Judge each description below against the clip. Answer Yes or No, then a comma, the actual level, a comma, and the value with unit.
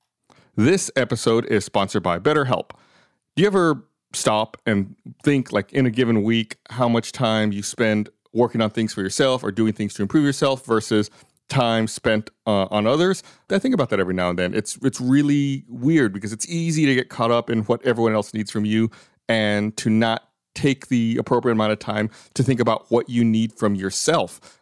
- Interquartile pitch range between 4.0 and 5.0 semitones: No, average, 3.5 semitones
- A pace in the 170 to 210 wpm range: Yes, average, 200 wpm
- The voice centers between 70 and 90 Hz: No, low, 115 Hz